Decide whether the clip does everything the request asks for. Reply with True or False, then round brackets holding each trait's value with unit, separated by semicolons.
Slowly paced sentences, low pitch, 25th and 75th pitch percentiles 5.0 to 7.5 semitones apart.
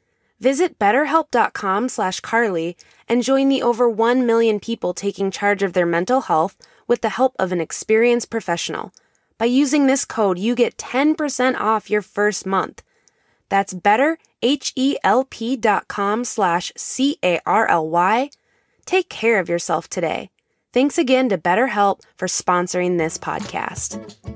False (130 wpm; 225 Hz; 5.4 semitones)